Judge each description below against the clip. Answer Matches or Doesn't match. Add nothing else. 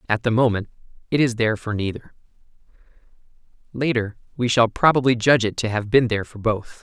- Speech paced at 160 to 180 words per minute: Matches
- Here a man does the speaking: Matches